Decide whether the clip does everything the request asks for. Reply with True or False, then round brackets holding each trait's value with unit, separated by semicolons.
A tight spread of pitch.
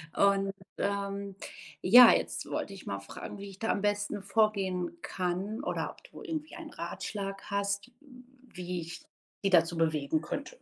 False (3.3 semitones)